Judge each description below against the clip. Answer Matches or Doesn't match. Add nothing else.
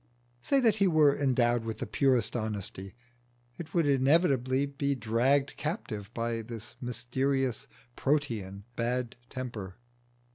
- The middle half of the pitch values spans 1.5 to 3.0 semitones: Doesn't match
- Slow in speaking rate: Matches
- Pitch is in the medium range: Doesn't match